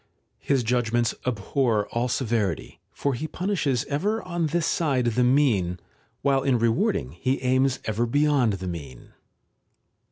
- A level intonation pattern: No, average, 4.0 semitones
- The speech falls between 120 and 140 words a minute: Yes, slow, 135 wpm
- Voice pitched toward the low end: Yes, low, 125 Hz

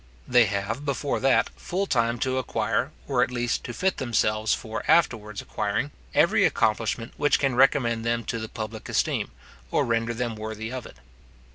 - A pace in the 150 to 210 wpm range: Yes, average, 170 wpm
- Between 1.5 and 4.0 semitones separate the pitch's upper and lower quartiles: Yes, average, 2.7 semitones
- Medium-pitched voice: No, low, 115 Hz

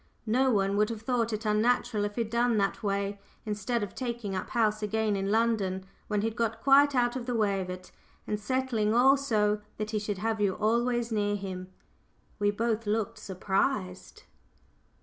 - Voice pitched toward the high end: Yes, high, 215 Hz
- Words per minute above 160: Yes, average, 185 wpm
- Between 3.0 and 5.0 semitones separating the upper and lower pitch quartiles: No, narrow, 2.5 semitones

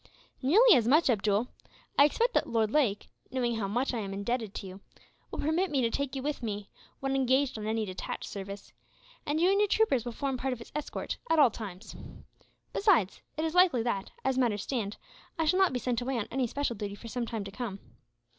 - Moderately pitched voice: No, high, 245 Hz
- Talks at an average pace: No, fast, 220 wpm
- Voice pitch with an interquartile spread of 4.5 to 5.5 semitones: Yes, average, 5.1 semitones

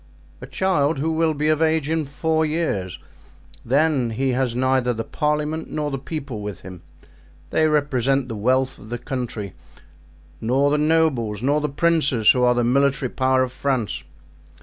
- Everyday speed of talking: Yes, average, 165 wpm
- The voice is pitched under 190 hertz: Yes, low, 135 Hz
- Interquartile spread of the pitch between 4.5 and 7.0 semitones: No, average, 3.9 semitones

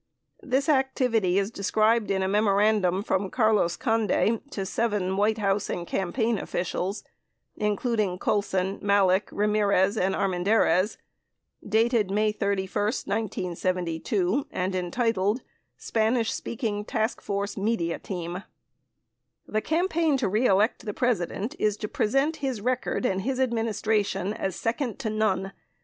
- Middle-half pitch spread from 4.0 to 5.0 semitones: No, average, 3.0 semitones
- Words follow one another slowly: Yes, slow, 125 wpm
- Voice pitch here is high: Yes, high, 210 Hz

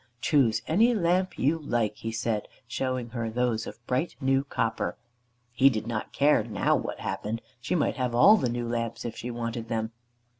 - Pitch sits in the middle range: No, low, 120 Hz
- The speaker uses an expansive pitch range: No, average, 3.0 semitones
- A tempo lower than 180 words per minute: No, average, 185 wpm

